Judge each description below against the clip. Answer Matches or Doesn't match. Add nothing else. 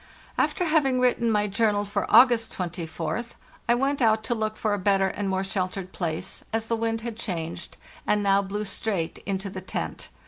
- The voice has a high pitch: Matches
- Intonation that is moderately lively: Matches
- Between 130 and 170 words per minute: Doesn't match